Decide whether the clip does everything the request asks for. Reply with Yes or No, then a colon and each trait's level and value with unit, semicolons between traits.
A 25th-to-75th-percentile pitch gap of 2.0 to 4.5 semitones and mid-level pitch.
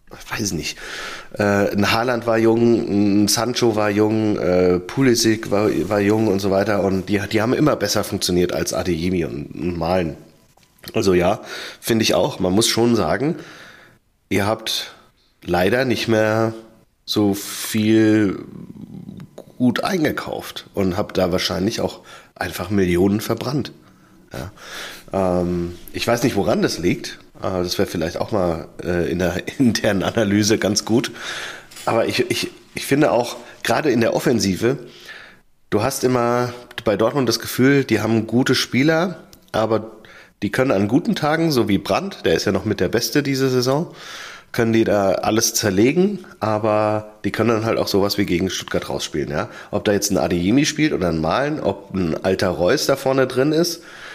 No: average, 3.4 semitones; low, 110 Hz